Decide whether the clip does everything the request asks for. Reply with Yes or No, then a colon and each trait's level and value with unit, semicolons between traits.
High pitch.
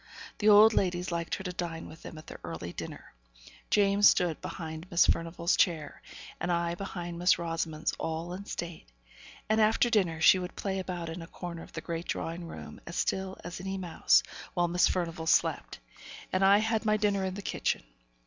No: medium, 175 Hz